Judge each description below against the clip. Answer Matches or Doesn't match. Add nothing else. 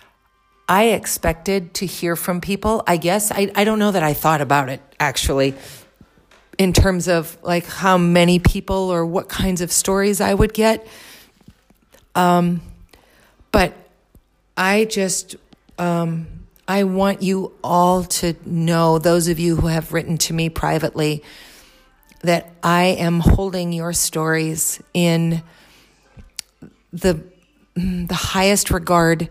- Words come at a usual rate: Doesn't match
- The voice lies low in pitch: Doesn't match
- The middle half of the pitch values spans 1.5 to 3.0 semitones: Matches